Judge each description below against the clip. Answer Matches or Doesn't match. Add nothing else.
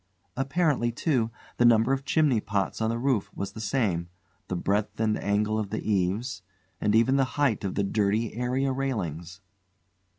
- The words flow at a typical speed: Matches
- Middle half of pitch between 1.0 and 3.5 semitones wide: Doesn't match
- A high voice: Doesn't match